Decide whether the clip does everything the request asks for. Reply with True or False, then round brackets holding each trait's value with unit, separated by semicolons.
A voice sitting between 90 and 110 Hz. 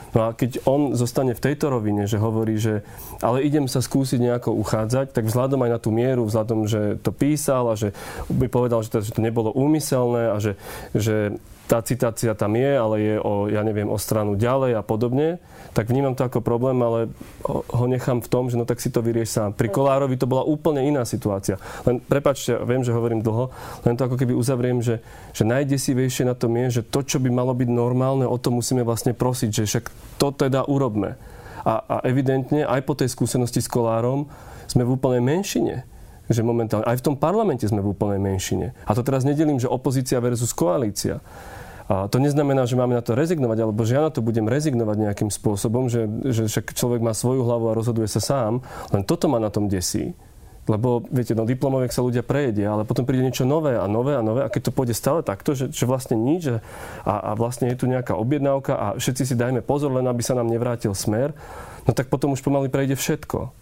False (125 Hz)